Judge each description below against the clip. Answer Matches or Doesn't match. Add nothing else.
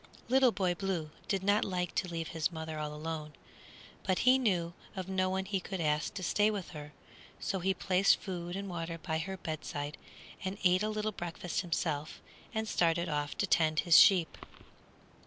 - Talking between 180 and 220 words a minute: Matches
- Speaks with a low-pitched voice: Doesn't match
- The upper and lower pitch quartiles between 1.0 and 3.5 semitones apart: Matches